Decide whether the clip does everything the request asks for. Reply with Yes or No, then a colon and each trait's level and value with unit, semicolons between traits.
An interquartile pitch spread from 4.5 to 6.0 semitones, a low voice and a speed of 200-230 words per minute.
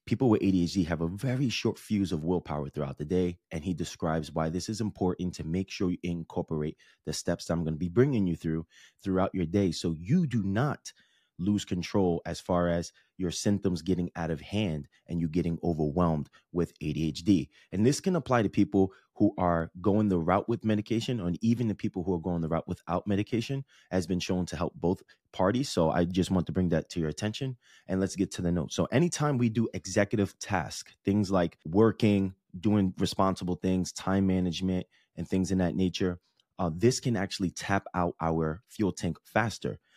No: average, 3.2 semitones; very low, 90 Hz; fast, 205 wpm